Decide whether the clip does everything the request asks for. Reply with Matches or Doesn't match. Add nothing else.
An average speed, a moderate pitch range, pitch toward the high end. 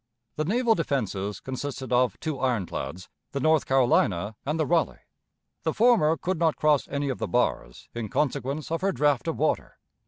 Doesn't match